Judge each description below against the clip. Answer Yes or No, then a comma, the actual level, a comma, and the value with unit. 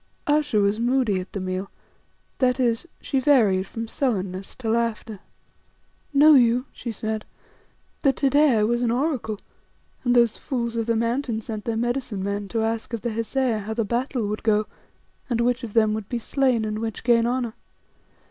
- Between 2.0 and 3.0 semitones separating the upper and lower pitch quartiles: Yes, narrow, 2.6 semitones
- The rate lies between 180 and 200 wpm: Yes, average, 185 wpm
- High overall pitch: Yes, high, 230 Hz